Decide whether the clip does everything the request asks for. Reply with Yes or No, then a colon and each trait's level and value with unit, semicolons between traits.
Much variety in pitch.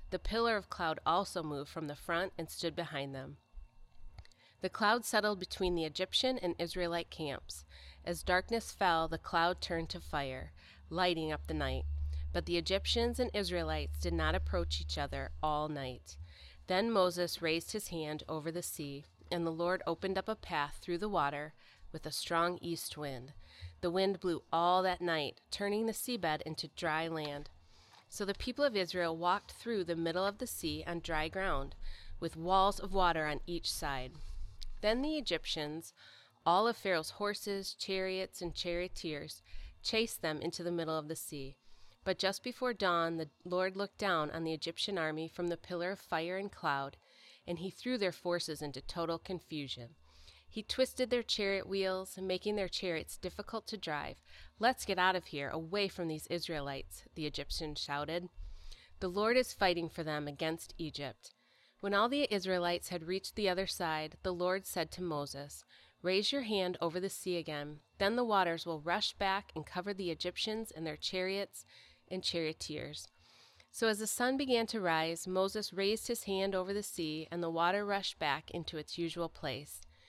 No: average, 4.3 semitones